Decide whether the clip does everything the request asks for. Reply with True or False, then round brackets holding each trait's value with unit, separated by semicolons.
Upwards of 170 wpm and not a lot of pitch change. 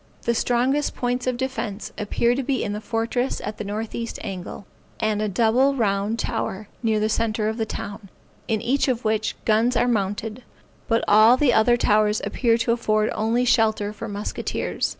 True (180 wpm; 2.2 semitones)